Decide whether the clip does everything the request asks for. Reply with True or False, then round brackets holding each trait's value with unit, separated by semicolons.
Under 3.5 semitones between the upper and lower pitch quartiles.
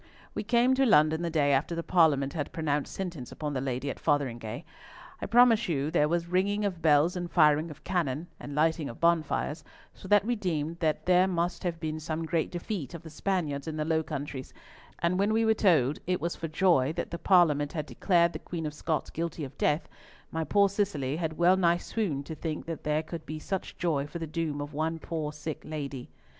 True (3.0 semitones)